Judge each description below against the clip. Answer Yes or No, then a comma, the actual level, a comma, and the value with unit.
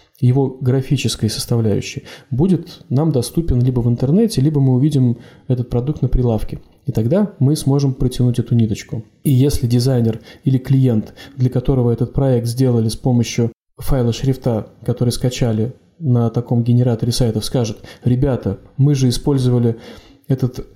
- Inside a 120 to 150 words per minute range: Yes, average, 140 wpm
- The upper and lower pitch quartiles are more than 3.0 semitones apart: No, narrow, 2.5 semitones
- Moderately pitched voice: No, low, 125 Hz